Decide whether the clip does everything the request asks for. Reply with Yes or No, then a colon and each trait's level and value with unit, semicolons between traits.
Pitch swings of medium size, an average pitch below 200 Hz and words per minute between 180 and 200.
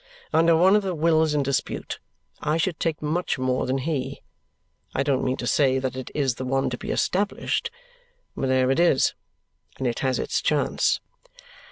Yes: average, 3.8 semitones; medium, 140 Hz; average, 185 wpm